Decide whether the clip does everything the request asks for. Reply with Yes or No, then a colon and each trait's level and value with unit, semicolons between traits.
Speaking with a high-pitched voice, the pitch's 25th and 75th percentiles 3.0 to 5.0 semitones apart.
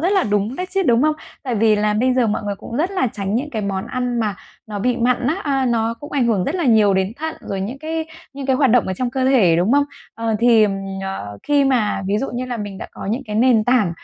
Yes: high, 240 Hz; average, 4.4 semitones